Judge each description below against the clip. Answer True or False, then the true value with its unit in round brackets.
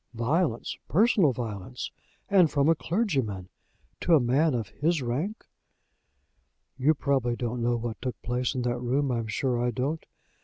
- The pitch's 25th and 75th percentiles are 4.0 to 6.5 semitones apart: True (4.6 semitones)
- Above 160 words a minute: False (155 wpm)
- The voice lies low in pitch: True (125 Hz)